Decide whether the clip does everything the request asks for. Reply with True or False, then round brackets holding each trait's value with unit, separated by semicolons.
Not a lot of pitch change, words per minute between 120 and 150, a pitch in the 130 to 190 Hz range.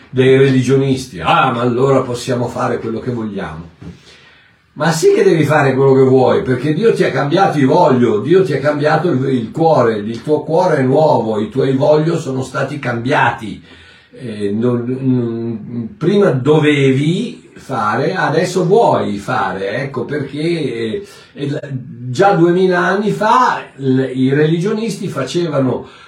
False (4.4 semitones; 130 wpm; 135 Hz)